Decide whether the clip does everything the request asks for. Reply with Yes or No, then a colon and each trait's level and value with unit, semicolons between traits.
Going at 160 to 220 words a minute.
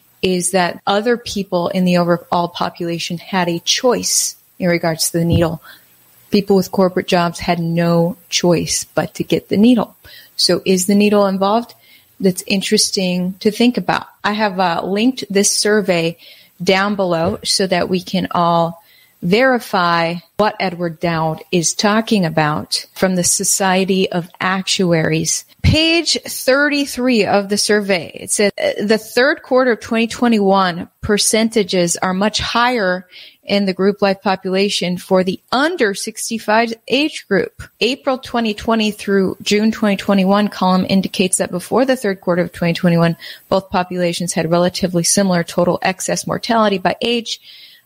No: average, 145 wpm